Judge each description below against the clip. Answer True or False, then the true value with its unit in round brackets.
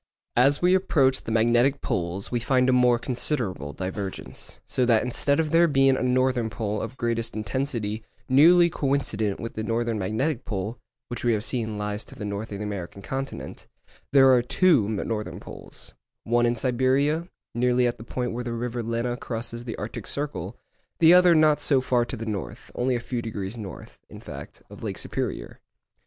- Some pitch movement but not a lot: True (3.4 semitones)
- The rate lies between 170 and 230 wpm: True (185 wpm)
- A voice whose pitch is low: True (120 Hz)